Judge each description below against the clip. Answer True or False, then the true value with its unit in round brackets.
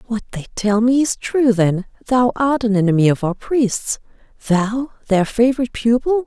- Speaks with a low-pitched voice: False (230 Hz)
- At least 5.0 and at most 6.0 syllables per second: False (4.8 syllables/s)